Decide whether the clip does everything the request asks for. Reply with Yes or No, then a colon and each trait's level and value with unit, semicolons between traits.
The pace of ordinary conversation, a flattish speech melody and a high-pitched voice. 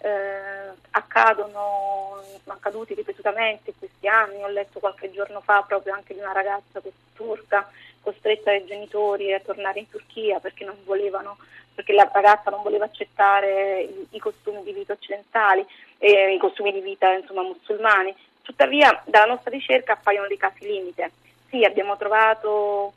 Yes: average, 155 wpm; narrow, 1.4 semitones; high, 205 Hz